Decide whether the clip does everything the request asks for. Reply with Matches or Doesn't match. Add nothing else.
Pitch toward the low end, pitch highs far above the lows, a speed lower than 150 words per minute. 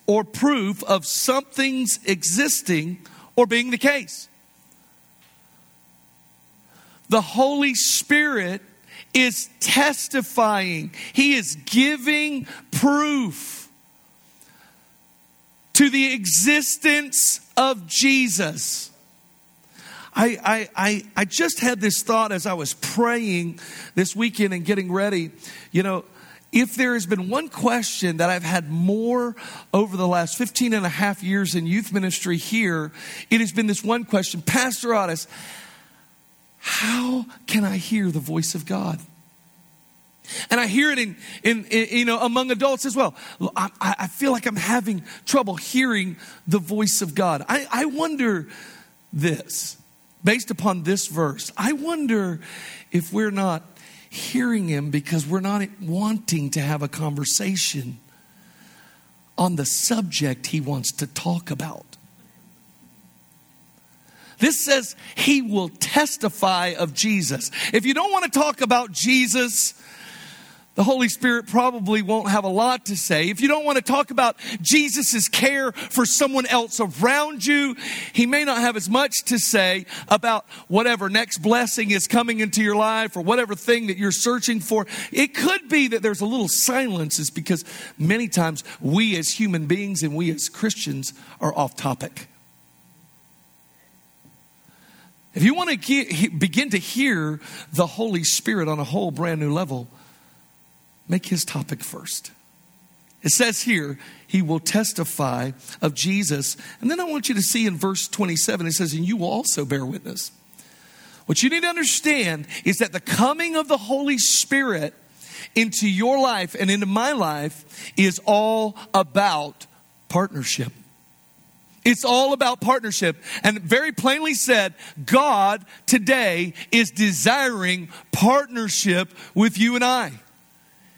Doesn't match